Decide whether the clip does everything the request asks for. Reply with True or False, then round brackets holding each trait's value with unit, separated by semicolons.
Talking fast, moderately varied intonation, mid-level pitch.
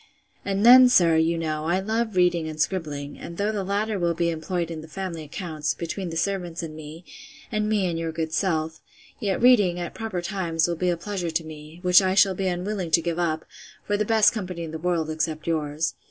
True (225 wpm; 3.3 semitones; 175 Hz)